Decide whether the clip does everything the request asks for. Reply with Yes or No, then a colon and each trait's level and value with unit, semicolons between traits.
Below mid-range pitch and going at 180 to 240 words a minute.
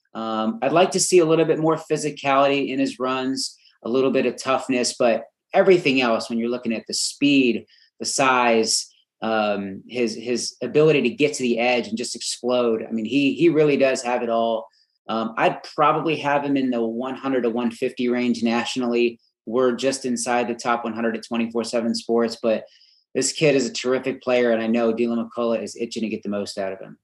Yes: low, 120 Hz; fast, 205 wpm